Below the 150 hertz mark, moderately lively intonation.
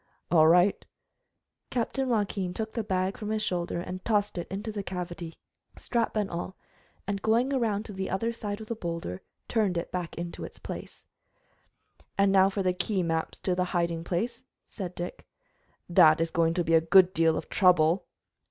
No: medium, 185 Hz; average, 3.5 semitones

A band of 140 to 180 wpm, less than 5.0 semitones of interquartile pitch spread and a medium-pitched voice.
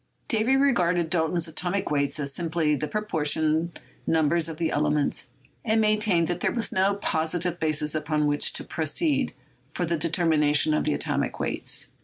Yes: average, 160 wpm; average, 3.1 semitones; medium, 165 Hz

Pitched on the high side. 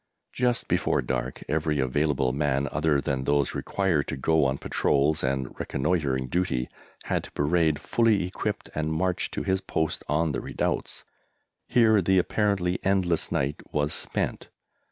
No: very low, 75 Hz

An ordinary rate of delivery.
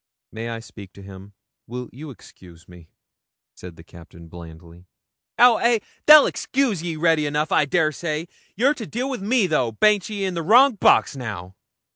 Yes: average, 175 wpm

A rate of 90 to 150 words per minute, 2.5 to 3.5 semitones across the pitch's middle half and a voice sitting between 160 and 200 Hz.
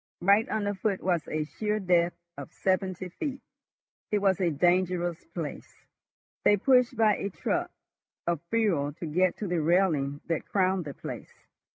No: average, 160 wpm; average, 3.2 semitones; medium, 185 Hz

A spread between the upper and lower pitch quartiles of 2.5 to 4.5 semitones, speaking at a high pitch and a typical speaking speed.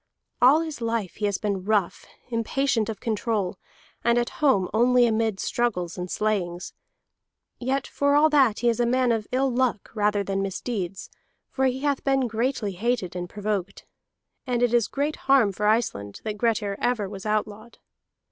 Yes: average, 3.6 semitones; high, 225 Hz; average, 170 wpm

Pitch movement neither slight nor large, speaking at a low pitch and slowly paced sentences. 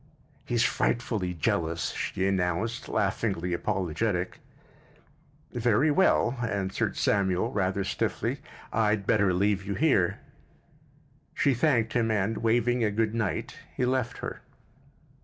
Yes: average, 3.9 semitones; low, 105 Hz; slow, 115 wpm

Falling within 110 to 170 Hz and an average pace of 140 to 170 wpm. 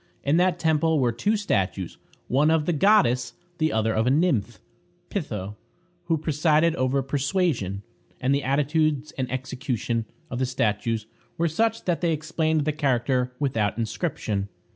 Yes: medium, 140 Hz; average, 150 wpm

